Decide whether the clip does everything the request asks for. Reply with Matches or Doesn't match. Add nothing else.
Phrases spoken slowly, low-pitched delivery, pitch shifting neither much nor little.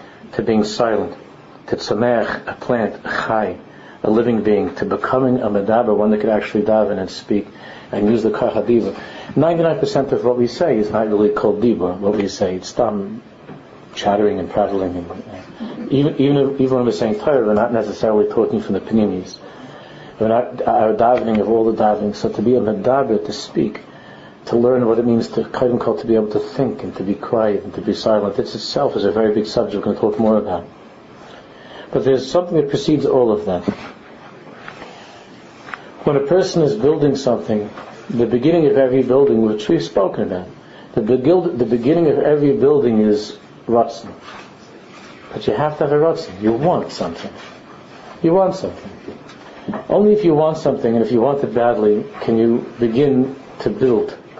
Doesn't match